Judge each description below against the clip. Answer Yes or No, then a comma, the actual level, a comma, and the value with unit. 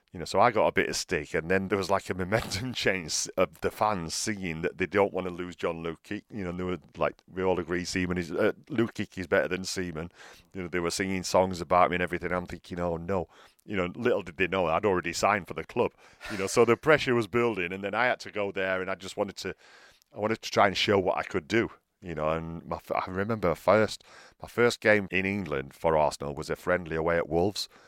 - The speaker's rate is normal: No, fast, 260 wpm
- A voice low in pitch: Yes, very low, 95 Hz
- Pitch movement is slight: Yes, narrow, 2.3 semitones